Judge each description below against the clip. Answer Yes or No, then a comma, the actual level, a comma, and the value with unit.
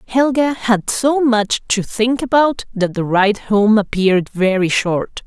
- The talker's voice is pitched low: No, high, 220 Hz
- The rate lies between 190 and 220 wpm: No, average, 160 wpm